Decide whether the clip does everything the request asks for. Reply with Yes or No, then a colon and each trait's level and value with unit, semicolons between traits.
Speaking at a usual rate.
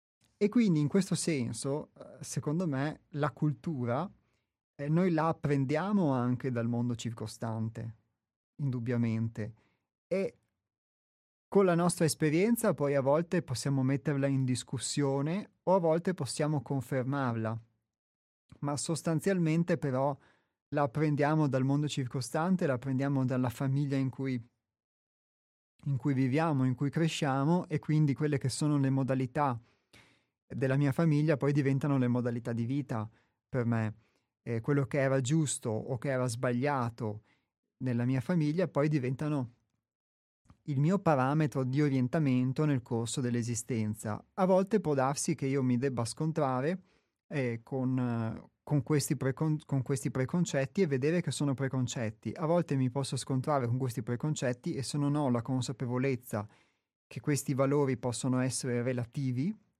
Yes: average, 140 wpm